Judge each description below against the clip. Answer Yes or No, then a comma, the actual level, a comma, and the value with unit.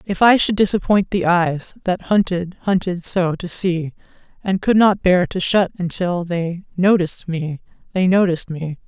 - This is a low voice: No, medium, 180 Hz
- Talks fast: No, average, 170 wpm